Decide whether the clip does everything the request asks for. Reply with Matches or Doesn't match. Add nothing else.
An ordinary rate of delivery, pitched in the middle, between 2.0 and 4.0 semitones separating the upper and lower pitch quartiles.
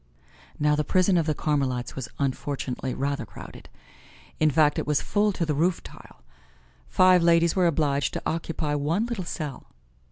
Matches